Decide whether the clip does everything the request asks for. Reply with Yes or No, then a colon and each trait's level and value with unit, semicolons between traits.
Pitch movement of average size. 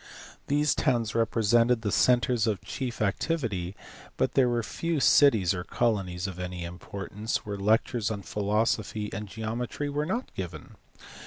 Yes: average, 3.9 semitones